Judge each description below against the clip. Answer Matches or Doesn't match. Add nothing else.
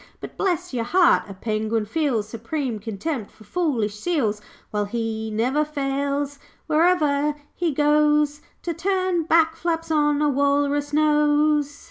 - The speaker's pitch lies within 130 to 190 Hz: Doesn't match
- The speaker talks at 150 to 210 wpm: Doesn't match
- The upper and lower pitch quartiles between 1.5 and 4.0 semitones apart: Doesn't match